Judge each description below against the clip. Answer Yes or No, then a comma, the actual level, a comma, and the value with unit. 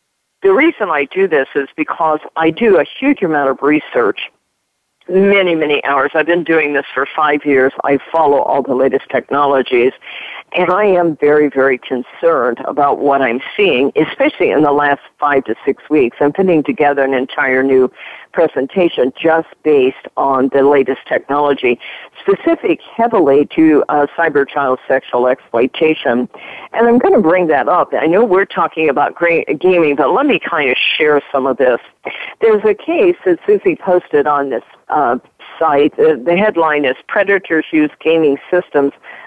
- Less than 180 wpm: Yes, average, 170 wpm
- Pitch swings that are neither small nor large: No, wide, 6.5 semitones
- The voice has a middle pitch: Yes, medium, 155 Hz